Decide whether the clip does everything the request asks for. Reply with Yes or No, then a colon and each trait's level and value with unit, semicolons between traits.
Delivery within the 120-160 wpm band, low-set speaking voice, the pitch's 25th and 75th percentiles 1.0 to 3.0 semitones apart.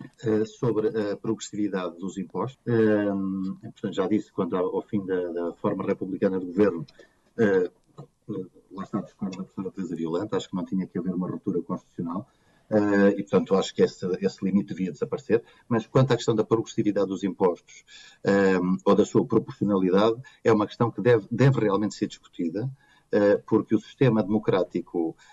No: average, 175 wpm; low, 105 Hz; narrow, 2.6 semitones